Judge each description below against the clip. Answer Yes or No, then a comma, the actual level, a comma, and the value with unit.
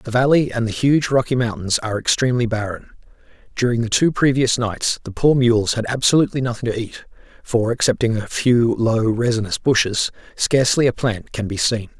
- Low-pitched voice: Yes, low, 120 Hz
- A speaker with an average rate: Yes, average, 180 wpm